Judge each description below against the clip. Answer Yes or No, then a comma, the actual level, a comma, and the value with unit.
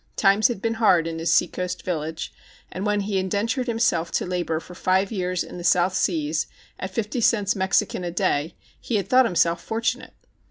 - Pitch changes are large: No, average, 3.6 semitones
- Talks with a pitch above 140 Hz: Yes, medium, 185 Hz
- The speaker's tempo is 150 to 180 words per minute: No, average, 190 wpm